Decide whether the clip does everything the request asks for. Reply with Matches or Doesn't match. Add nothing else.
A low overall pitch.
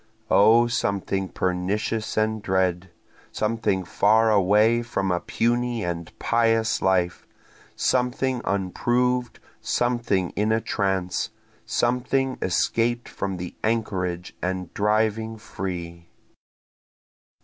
Matches